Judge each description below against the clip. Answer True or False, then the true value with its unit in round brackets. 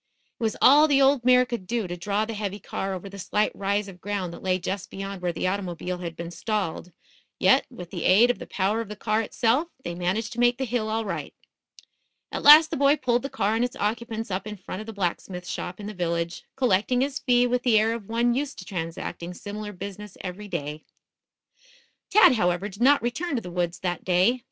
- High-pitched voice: True (210 Hz)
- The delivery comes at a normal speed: False (230 wpm)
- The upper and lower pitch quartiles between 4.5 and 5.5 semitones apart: True (4.8 semitones)